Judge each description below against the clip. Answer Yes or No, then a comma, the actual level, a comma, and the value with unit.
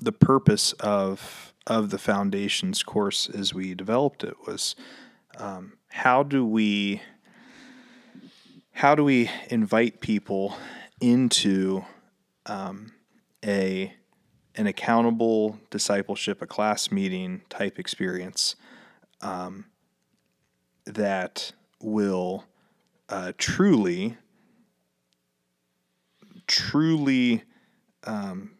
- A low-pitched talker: Yes, low, 110 Hz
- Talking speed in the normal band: No, slow, 80 wpm